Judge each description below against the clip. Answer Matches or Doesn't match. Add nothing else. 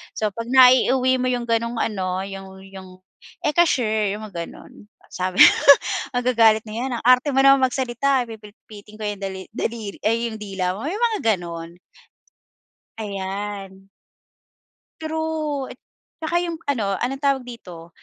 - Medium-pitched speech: Doesn't match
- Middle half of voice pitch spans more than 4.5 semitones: Matches